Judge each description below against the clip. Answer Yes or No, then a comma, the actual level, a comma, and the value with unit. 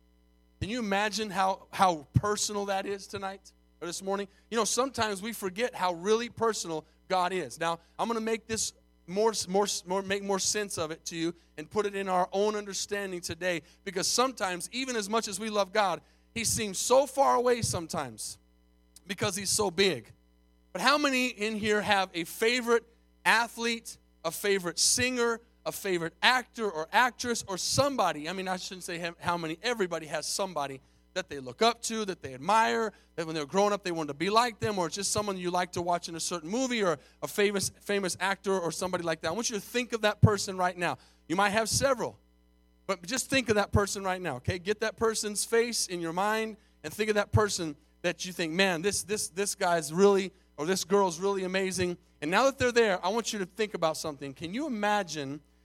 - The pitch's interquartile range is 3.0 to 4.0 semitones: No, average, 4.4 semitones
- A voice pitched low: No, high, 195 Hz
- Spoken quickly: Yes, fast, 215 wpm